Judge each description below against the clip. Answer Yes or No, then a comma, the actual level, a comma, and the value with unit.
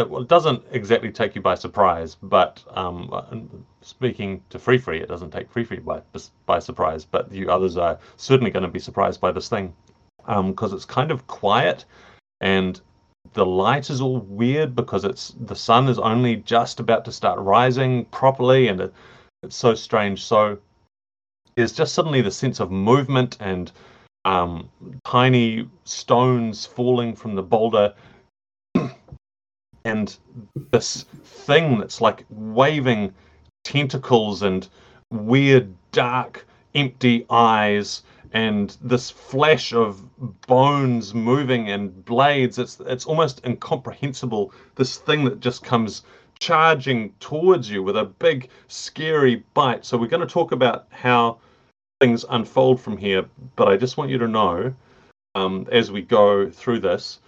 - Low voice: Yes, low, 115 Hz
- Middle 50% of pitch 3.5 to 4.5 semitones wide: Yes, average, 4.2 semitones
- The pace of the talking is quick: No, average, 145 wpm